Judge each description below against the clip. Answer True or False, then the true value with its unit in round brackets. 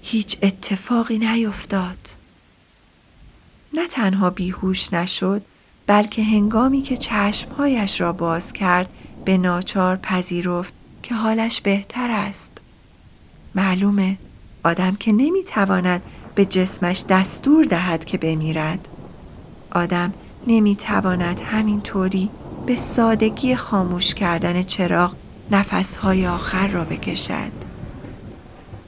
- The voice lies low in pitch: False (195 Hz)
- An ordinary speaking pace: False (90 wpm)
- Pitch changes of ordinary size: True (3.3 semitones)